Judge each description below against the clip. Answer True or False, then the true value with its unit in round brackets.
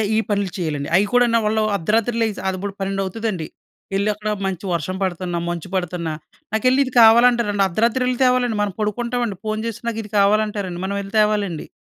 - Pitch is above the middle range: True (210 Hz)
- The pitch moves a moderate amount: True (3.2 semitones)